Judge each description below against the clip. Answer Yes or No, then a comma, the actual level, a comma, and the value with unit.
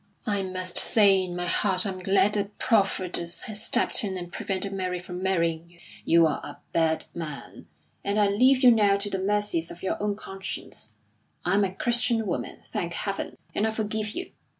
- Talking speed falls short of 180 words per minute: No, average, 195 wpm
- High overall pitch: Yes, high, 195 Hz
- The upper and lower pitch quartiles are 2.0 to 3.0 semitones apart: Yes, average, 2.7 semitones